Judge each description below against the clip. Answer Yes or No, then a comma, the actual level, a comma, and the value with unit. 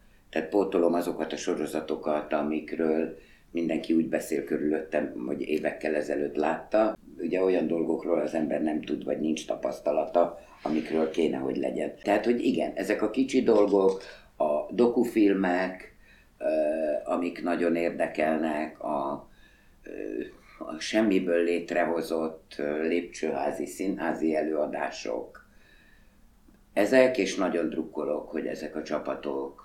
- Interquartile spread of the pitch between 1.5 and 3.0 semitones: No, average, 3.7 semitones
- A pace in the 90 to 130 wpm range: Yes, average, 110 wpm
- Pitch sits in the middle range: No, very low, 85 Hz